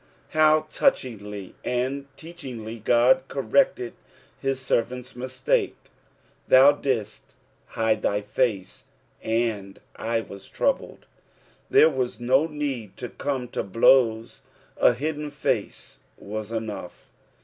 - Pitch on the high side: No, low, 125 Hz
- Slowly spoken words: Yes, slow, 105 wpm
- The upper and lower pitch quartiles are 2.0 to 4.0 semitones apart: Yes, average, 3.5 semitones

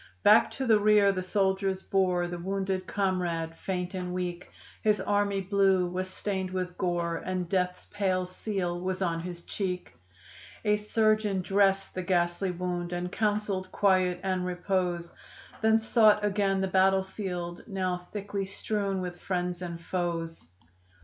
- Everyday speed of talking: Yes, average, 145 wpm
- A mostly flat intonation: Yes, narrow, 1.8 semitones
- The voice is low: No, medium, 185 Hz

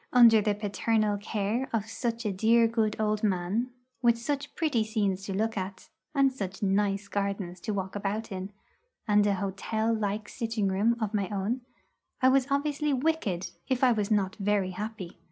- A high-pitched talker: Yes, high, 215 Hz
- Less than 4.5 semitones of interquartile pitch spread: Yes, average, 2.9 semitones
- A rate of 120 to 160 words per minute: No, average, 175 wpm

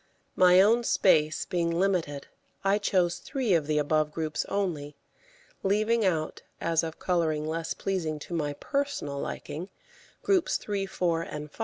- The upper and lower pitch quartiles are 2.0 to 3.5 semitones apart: No, average, 4.0 semitones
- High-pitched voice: No, medium, 170 Hz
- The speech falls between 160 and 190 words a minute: No, average, 150 wpm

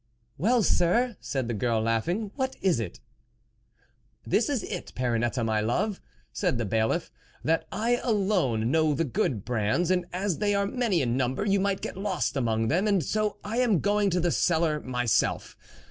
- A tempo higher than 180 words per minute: Yes, average, 190 wpm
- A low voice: No, medium, 170 Hz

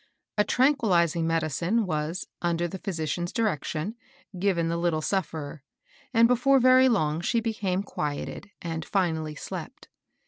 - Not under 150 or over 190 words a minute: No, average, 140 wpm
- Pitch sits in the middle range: Yes, medium, 175 Hz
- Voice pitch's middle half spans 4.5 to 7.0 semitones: Yes, average, 5.1 semitones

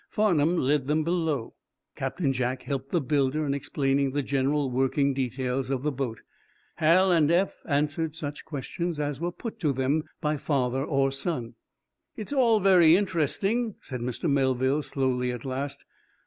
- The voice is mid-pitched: Yes, medium, 145 Hz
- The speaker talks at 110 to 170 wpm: Yes, average, 160 wpm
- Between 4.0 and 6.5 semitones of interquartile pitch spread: No, average, 3.5 semitones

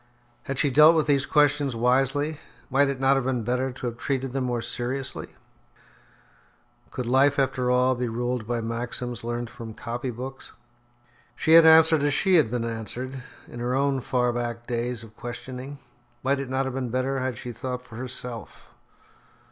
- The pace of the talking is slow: No, average, 180 wpm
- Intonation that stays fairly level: Yes, narrow, 2.1 semitones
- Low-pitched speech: Yes, low, 125 Hz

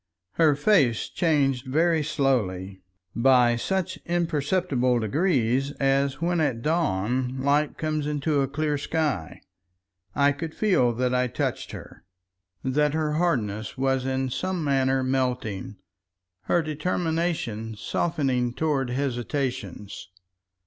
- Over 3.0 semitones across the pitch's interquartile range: Yes, average, 4.1 semitones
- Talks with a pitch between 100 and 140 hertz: Yes, low, 135 Hz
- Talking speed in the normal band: No, slow, 110 wpm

